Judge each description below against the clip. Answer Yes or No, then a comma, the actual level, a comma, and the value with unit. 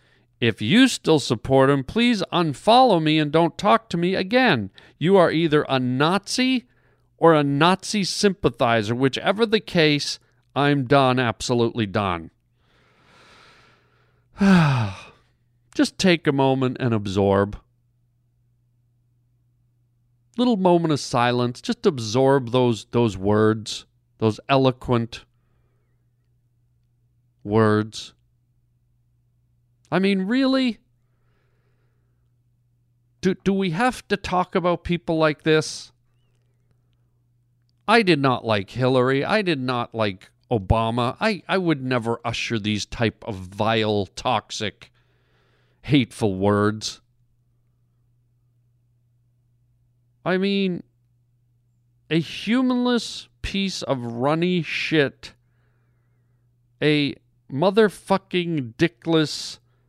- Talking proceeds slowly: Yes, slow, 95 wpm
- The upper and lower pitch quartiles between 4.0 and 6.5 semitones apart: Yes, average, 5.1 semitones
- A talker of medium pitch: No, low, 120 Hz